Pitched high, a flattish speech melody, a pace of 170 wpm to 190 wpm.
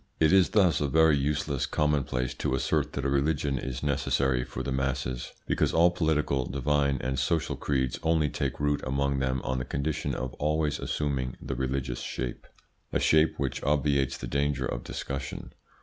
No: very low, 70 Hz; narrow, 2.2 semitones; average, 175 wpm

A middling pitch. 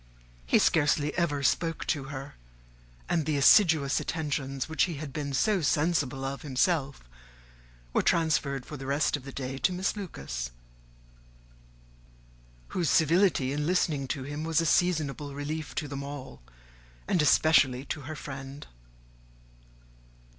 Yes: medium, 145 Hz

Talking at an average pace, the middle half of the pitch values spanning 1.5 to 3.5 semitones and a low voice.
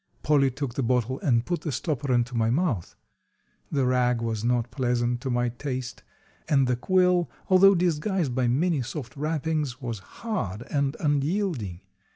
No: average, 160 wpm; average, 4.2 semitones; low, 130 Hz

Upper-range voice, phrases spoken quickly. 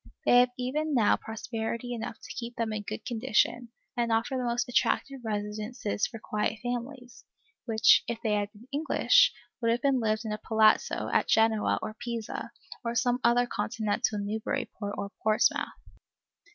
No: high, 230 Hz; average, 160 wpm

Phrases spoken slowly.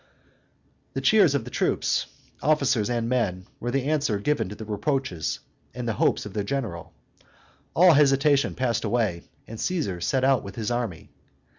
No: average, 160 wpm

